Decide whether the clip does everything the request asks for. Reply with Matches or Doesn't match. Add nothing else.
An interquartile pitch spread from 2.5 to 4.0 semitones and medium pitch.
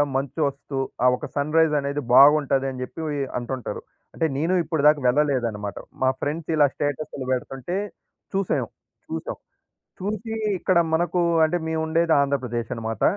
Matches